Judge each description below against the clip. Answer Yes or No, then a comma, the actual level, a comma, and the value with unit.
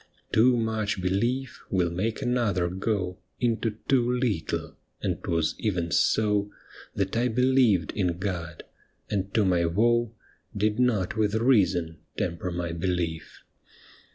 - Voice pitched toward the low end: Yes, low, 100 Hz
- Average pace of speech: No, slow, 125 wpm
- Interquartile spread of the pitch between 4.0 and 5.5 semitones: Yes, average, 4.7 semitones